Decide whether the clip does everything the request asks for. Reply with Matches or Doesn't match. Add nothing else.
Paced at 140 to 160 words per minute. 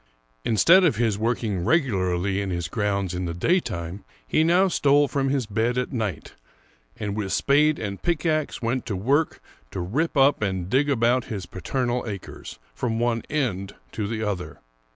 Doesn't match